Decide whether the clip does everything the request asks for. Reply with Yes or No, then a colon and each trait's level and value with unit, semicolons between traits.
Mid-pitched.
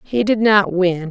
No: high, 200 Hz